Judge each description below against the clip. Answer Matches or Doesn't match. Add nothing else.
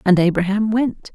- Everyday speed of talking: Matches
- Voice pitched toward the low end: Doesn't match